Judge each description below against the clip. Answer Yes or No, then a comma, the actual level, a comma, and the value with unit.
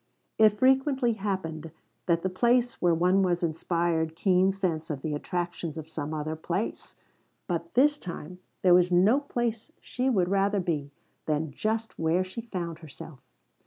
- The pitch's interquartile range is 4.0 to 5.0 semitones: Yes, average, 4.7 semitones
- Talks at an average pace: Yes, average, 160 wpm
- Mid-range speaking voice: Yes, medium, 180 Hz